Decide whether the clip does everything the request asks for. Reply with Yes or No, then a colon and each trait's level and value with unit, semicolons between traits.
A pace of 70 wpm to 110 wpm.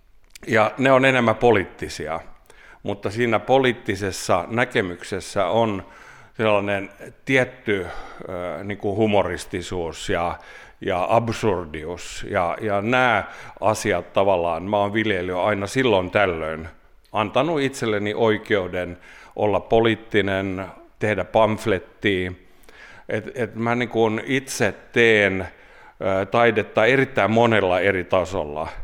Yes: average, 100 wpm